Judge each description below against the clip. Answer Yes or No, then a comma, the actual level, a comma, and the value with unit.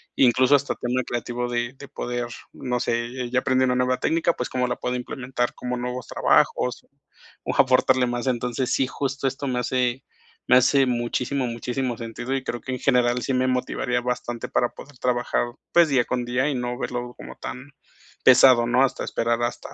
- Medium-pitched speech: No, low, 125 Hz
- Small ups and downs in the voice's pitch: Yes, narrow, 1.1 semitones